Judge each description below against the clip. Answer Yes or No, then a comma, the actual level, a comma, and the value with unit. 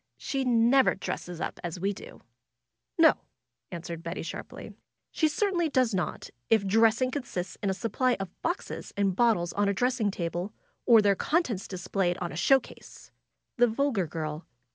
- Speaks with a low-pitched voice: No, high, 205 Hz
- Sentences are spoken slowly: No, average, 170 wpm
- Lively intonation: Yes, wide, 6.0 semitones